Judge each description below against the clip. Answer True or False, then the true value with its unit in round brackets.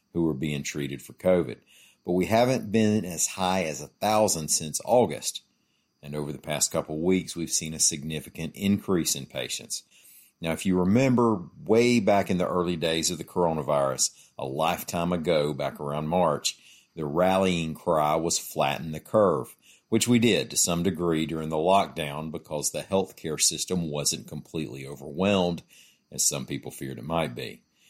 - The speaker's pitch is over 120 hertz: False (80 Hz)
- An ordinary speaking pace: True (170 wpm)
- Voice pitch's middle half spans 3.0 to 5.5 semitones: True (3.9 semitones)